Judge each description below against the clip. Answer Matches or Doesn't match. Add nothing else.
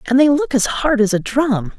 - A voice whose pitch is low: Doesn't match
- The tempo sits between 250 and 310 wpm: Matches